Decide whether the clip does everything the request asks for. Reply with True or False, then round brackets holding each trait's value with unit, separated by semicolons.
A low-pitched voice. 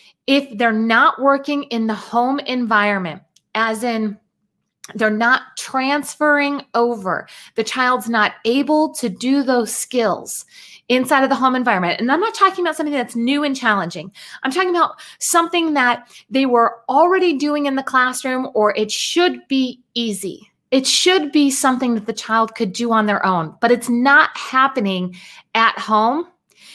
False (250 Hz)